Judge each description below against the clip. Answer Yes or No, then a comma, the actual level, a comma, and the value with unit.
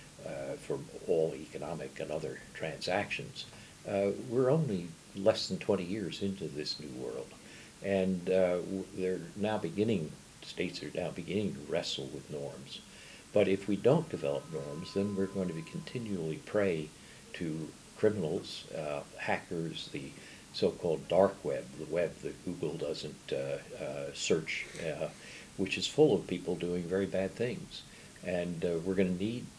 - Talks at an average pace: Yes, average, 150 wpm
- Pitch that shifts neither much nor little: No, narrow, 2.0 semitones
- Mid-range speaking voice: No, very low, 95 Hz